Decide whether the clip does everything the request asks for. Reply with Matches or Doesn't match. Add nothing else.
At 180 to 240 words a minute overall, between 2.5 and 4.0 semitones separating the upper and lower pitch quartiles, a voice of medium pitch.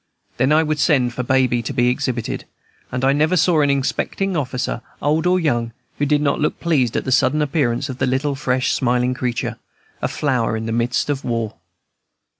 Doesn't match